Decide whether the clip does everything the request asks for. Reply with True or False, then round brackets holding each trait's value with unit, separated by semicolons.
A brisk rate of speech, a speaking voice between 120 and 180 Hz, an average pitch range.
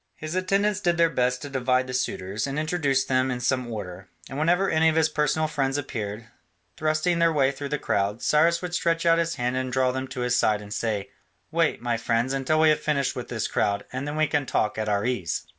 True (235 wpm; 135 Hz; 4.5 semitones)